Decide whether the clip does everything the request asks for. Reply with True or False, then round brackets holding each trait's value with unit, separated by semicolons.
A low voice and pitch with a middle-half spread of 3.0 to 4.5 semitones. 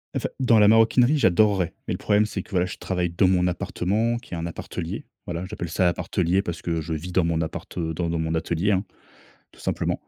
True (90 Hz; 3.6 semitones)